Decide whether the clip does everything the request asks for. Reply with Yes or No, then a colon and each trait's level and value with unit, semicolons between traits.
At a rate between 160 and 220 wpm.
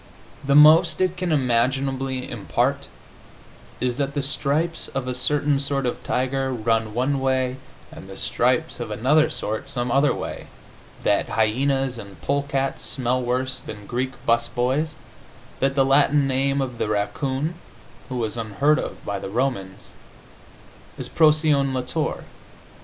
No: average, 145 wpm